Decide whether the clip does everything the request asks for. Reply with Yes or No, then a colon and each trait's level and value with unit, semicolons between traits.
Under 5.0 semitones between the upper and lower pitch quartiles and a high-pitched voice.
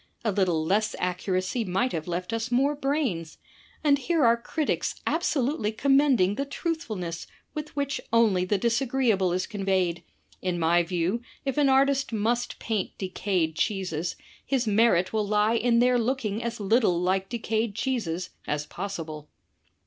No: wide, 5.4 semitones; high, 215 Hz